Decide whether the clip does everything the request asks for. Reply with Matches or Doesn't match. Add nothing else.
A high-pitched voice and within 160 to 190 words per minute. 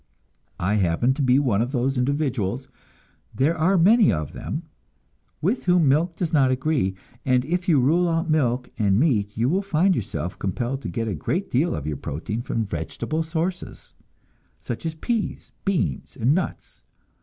Doesn't match